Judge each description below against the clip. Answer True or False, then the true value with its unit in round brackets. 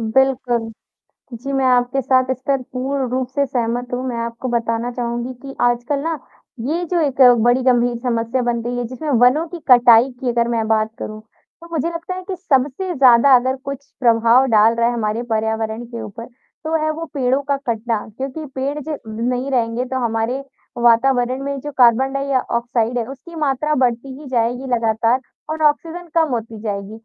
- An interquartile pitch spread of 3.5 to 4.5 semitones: False (2.8 semitones)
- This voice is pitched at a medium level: False (250 Hz)